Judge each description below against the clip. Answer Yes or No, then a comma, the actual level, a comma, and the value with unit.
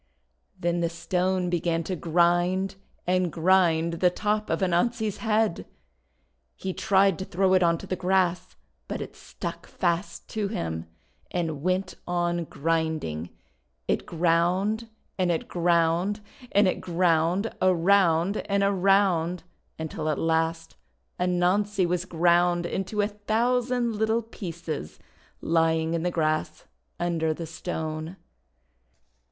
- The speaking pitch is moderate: Yes, medium, 175 Hz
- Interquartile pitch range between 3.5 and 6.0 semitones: No, average, 2.8 semitones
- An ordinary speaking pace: No, slow, 125 wpm